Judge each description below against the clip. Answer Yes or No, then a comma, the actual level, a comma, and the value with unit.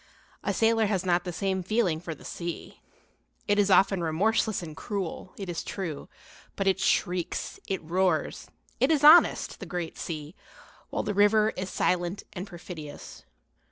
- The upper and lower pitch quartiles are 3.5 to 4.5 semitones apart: No, average, 3.1 semitones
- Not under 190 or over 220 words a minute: No, average, 160 wpm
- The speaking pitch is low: No, medium, 185 Hz